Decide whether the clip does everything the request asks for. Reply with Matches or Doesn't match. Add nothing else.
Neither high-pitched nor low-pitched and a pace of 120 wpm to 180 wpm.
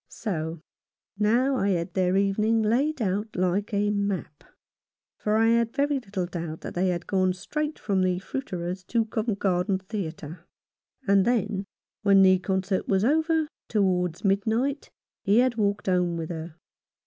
Doesn't match